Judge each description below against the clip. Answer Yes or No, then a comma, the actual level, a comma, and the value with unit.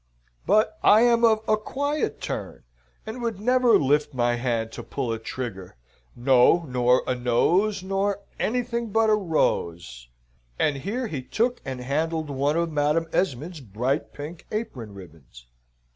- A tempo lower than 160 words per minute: Yes, average, 150 wpm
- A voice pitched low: No, medium, 150 Hz